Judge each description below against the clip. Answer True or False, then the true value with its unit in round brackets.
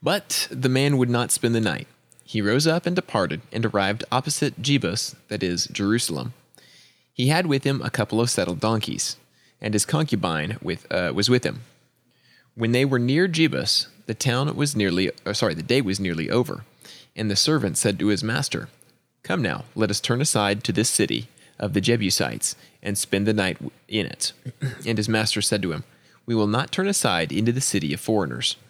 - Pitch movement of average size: True (4.4 semitones)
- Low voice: True (115 Hz)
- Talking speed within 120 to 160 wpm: False (195 wpm)